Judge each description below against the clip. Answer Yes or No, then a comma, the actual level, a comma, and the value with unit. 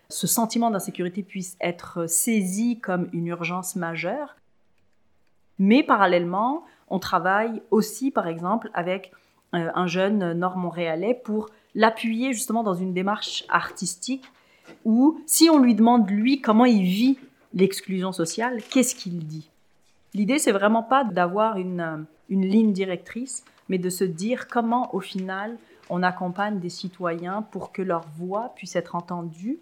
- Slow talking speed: Yes, slow, 140 wpm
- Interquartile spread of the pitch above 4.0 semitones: Yes, average, 4.5 semitones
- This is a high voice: Yes, high, 195 Hz